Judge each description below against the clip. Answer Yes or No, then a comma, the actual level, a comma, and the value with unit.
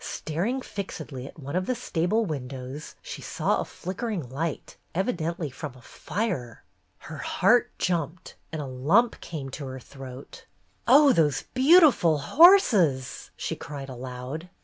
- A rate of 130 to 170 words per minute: Yes, average, 140 wpm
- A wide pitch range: Yes, wide, 7.0 semitones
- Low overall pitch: No, medium, 160 Hz